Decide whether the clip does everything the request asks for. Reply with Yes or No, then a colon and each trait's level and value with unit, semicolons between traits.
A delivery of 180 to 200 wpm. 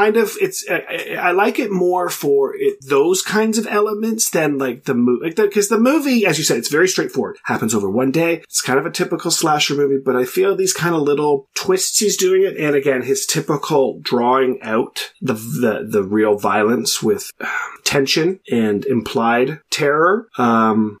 Yes: average, 195 wpm